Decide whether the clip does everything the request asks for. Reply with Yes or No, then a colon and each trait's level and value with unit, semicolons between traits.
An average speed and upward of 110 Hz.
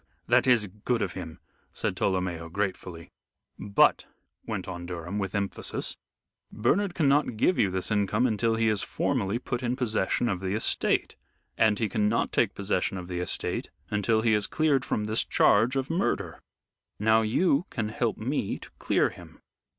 No: average, 165 wpm; low, 105 Hz